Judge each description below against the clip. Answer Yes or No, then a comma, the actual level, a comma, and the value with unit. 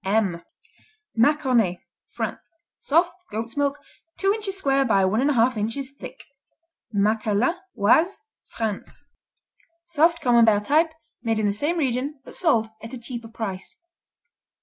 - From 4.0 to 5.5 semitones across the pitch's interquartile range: Yes, average, 5.1 semitones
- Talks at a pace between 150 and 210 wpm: No, slow, 135 wpm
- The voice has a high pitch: Yes, high, 240 Hz